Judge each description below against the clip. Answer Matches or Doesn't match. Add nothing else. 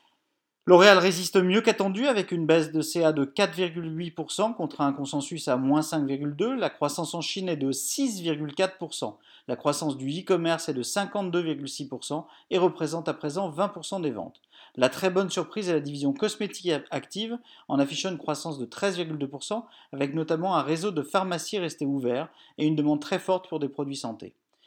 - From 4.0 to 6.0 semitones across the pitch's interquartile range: Matches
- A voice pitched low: Doesn't match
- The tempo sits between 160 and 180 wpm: Matches